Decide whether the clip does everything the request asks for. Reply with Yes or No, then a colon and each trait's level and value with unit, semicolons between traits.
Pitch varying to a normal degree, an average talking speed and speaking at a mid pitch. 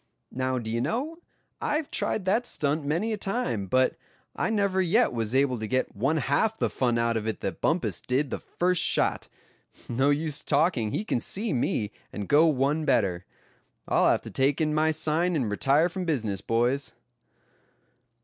No: wide, 6.8 semitones; average, 180 wpm; medium, 145 Hz